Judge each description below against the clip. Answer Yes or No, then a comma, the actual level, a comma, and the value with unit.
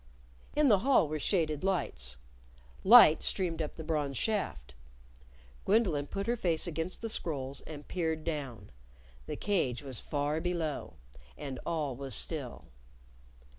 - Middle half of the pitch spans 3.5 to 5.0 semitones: Yes, average, 4.6 semitones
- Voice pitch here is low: No, medium, 155 Hz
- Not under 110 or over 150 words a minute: Yes, slow, 135 wpm